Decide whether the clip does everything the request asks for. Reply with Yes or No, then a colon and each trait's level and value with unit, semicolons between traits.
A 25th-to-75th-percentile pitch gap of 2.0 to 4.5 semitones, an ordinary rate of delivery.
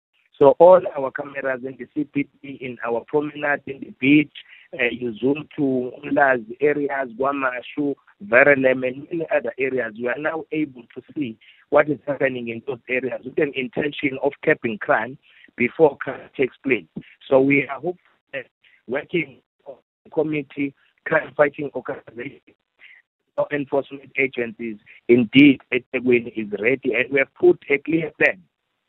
Yes: average, 2.8 semitones; average, 150 wpm